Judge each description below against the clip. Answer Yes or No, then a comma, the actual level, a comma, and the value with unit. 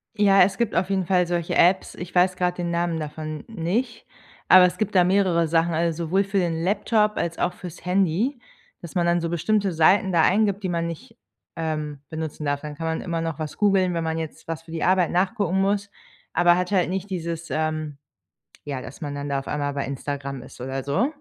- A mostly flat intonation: No, average, 3.2 semitones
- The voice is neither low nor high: Yes, medium, 170 Hz